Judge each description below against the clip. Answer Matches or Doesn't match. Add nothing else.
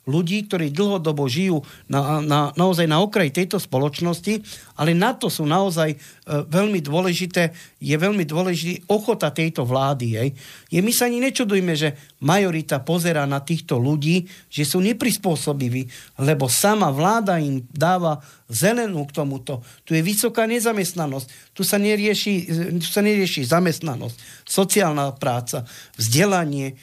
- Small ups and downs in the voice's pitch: Doesn't match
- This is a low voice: Doesn't match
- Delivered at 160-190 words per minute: Doesn't match